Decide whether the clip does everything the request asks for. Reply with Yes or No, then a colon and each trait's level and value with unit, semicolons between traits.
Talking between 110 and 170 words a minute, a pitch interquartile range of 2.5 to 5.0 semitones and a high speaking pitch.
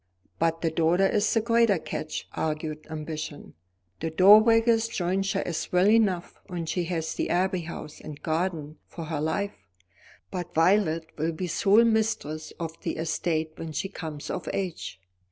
No: average, 155 wpm; average, 3.6 semitones; medium, 170 Hz